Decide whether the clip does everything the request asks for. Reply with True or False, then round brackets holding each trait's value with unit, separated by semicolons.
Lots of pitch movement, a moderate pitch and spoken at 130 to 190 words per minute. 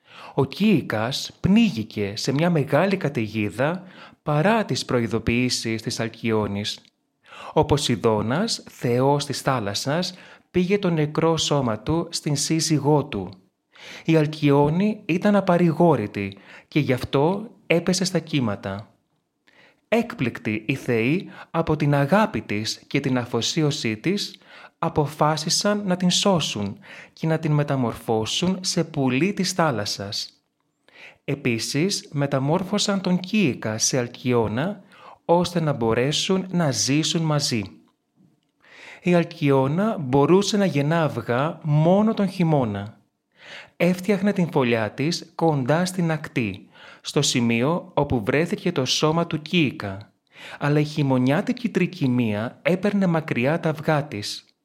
False (6.3 semitones; 150 Hz; 115 wpm)